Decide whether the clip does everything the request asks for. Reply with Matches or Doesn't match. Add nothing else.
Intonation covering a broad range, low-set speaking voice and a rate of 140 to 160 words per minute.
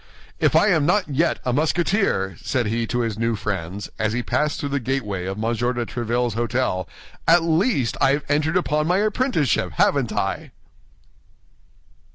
Doesn't match